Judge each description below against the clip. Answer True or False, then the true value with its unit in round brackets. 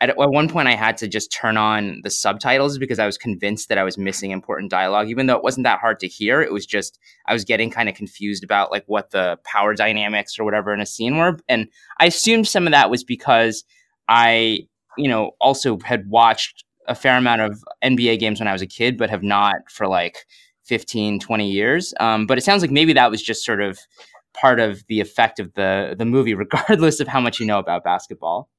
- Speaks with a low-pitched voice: True (110 Hz)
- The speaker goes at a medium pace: False (230 wpm)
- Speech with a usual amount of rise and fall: True (3.5 semitones)